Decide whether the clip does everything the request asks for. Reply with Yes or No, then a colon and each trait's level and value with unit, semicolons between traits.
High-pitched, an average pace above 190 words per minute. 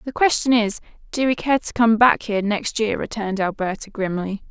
Yes: high, 220 Hz; average, 200 wpm